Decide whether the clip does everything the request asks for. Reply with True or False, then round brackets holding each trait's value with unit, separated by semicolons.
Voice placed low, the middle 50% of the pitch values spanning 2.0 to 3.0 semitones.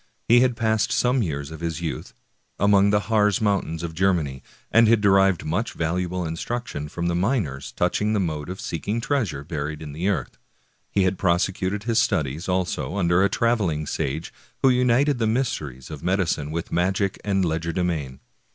False (90 Hz; 4.7 semitones)